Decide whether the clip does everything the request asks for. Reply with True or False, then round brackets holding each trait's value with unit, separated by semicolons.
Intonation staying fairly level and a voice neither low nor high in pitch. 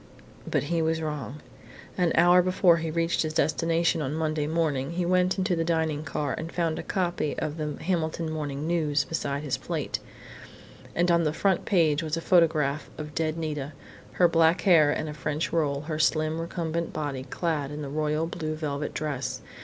True (2.0 semitones; 160 Hz)